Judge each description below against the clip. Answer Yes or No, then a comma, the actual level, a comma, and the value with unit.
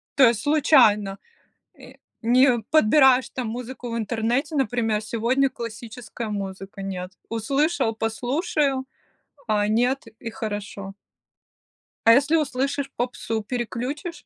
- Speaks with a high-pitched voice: Yes, high, 240 Hz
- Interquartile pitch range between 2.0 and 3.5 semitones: No, average, 3.9 semitones